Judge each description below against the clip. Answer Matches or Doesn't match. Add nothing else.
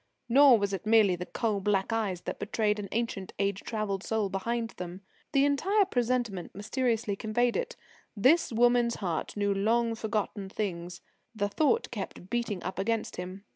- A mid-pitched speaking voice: Doesn't match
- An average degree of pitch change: Matches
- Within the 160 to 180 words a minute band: Matches